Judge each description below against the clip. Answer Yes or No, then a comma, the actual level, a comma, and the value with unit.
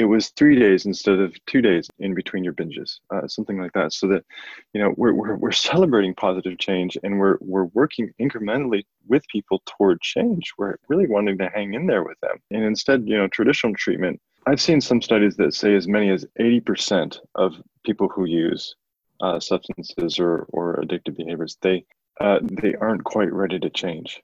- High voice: No, low, 100 Hz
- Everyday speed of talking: Yes, average, 195 wpm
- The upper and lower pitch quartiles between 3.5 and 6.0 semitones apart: No, average, 2.7 semitones